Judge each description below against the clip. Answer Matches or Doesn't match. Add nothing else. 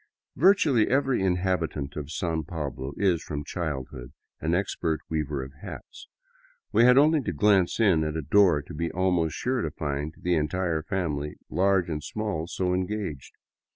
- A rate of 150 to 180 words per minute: Matches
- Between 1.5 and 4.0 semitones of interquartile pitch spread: Doesn't match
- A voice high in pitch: Doesn't match